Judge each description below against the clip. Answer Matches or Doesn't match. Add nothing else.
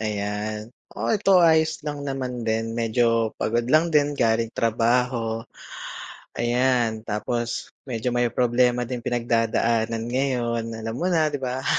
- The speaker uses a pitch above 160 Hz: Doesn't match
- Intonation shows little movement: Matches